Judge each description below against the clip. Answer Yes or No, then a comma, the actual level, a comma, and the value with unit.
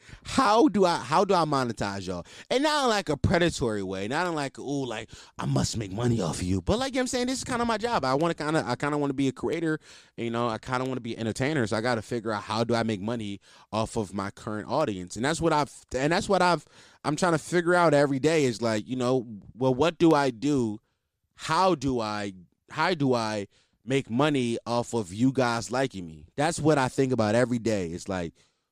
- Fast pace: Yes, fast, 265 wpm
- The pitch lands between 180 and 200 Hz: No, low, 130 Hz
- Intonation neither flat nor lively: No, wide, 5.9 semitones